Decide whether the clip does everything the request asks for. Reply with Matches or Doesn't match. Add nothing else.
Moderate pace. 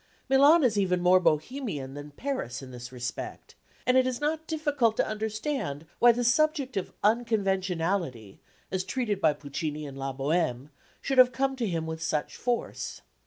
Matches